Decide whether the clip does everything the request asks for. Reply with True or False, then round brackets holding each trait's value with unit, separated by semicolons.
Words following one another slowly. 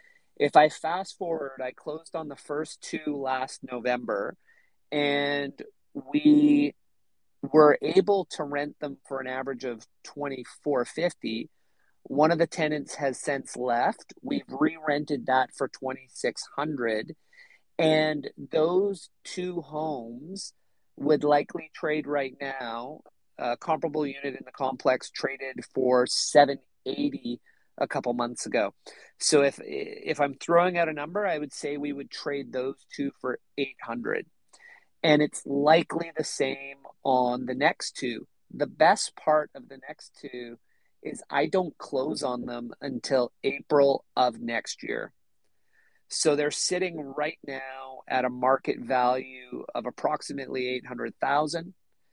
True (130 wpm)